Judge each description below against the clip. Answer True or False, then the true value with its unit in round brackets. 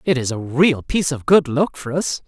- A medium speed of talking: False (265 wpm)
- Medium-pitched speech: True (145 Hz)